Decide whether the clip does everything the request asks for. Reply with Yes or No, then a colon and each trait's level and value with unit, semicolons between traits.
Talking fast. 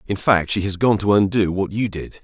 Yes: fast, 270 wpm